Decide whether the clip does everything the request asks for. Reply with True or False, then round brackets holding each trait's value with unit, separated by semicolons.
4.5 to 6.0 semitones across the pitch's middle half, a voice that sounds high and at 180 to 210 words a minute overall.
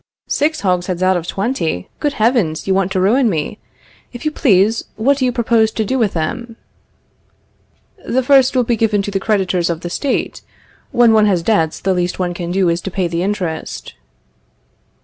True (4.9 semitones; 200 Hz; 190 wpm)